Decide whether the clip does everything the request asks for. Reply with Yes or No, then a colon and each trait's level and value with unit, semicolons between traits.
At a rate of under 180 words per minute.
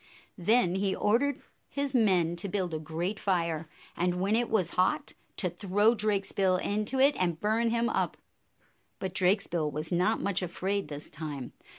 Yes: average, 165 wpm